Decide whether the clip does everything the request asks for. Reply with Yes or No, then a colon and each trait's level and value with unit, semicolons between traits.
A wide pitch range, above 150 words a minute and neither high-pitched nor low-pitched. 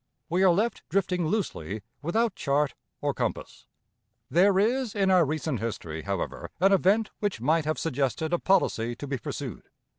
Yes: wide, 6.2 semitones; average, 160 wpm; medium, 170 Hz